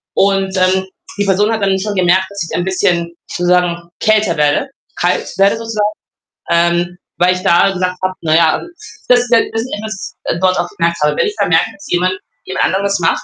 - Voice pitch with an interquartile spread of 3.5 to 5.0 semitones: No, narrow, 2.5 semitones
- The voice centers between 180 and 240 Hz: Yes, medium, 185 Hz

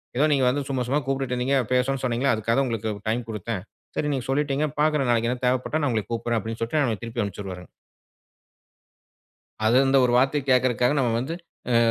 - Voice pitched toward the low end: Yes, low, 125 Hz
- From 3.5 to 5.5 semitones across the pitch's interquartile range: No, average, 2.9 semitones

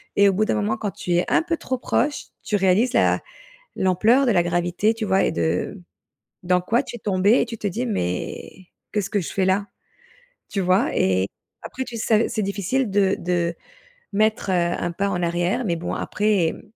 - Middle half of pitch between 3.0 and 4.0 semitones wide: Yes, average, 3.7 semitones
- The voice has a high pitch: Yes, high, 200 Hz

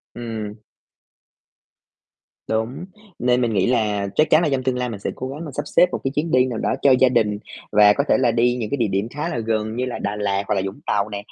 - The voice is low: Yes, low, 120 Hz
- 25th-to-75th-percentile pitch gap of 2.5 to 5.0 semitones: Yes, average, 3.6 semitones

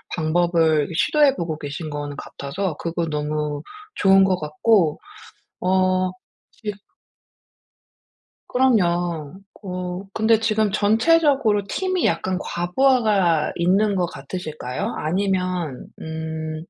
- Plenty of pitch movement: No, average, 4.6 semitones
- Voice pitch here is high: No, medium, 180 Hz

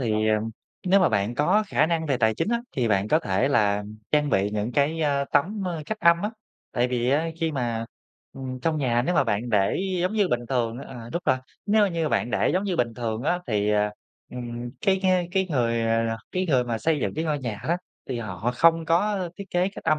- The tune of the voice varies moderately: No, wide, 6.6 semitones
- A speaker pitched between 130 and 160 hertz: Yes, low, 135 Hz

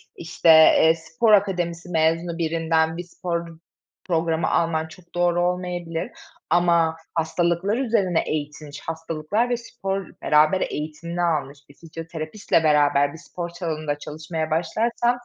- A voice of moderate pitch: Yes, medium, 165 Hz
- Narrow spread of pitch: Yes, narrow, 1.9 semitones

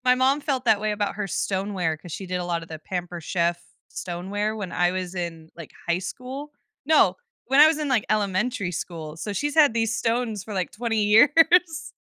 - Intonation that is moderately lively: No, wide, 6.0 semitones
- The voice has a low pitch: No, high, 205 Hz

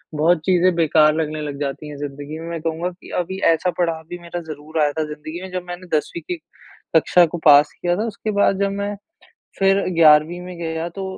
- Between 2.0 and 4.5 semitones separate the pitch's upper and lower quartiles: Yes, average, 2.8 semitones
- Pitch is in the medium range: Yes, medium, 165 Hz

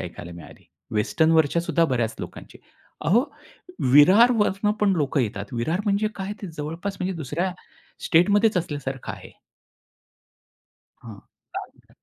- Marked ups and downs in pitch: Yes, wide, 6.6 semitones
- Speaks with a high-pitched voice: No, medium, 165 Hz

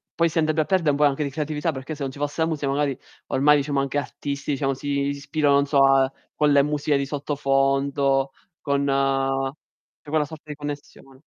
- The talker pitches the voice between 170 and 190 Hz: No, medium, 140 Hz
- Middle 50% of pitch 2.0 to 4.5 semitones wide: No, narrow, 1.4 semitones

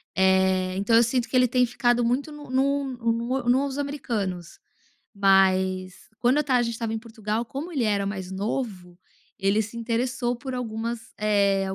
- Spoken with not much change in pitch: No, average, 4.3 semitones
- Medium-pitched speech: No, high, 230 Hz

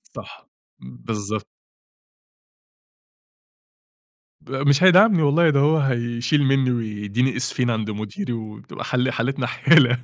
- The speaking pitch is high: No, low, 125 Hz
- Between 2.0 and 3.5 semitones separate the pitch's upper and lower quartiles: No, average, 4.3 semitones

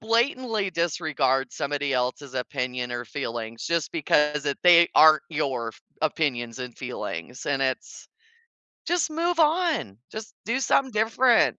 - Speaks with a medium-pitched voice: Yes, medium, 150 Hz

